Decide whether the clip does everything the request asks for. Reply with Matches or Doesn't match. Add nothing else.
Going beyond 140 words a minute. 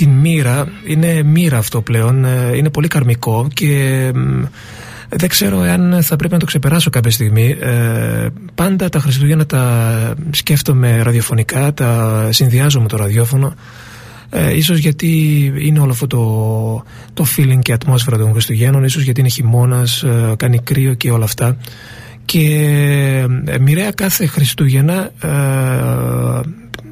Doesn't match